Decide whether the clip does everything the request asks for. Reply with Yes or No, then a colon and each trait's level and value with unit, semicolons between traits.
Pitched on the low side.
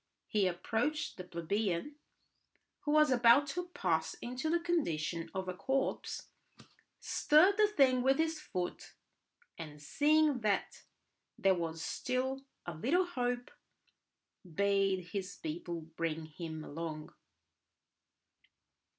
No: high, 200 Hz